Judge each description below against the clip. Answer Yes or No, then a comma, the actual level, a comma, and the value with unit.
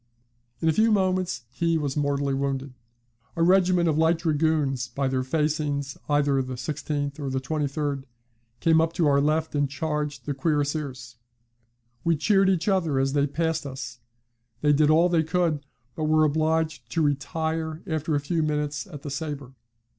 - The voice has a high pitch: No, medium, 150 Hz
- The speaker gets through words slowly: No, average, 165 wpm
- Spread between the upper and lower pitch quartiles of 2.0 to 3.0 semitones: Yes, narrow, 2.5 semitones